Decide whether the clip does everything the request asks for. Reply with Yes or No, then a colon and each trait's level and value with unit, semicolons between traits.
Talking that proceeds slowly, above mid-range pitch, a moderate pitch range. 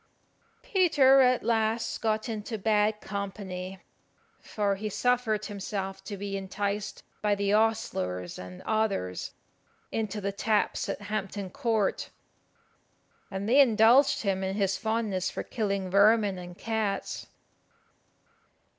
No: slow, 120 wpm; high, 210 Hz; narrow, 2.3 semitones